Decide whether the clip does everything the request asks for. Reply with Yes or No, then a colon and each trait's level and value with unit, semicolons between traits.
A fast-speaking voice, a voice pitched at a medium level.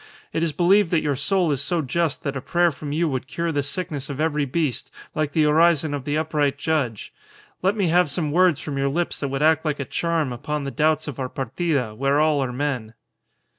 Yes: fast, 230 wpm; medium, 150 Hz